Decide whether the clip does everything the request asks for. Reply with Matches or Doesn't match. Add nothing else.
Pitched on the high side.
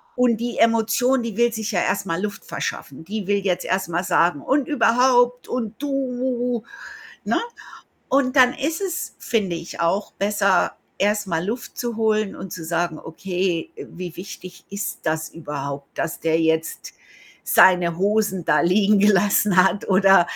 Matches